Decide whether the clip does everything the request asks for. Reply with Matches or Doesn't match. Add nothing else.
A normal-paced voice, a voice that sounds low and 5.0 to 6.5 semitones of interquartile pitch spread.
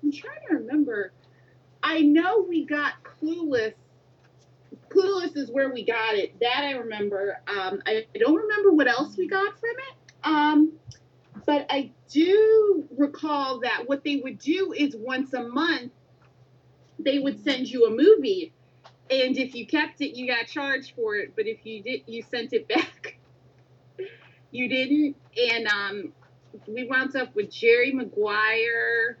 Doesn't match